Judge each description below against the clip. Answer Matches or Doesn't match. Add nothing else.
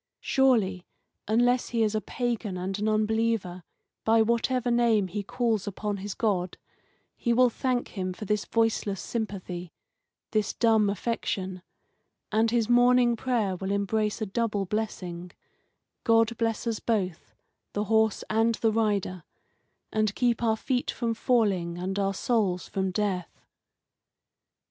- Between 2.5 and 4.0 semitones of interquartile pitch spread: Matches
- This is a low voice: Doesn't match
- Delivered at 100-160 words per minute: Matches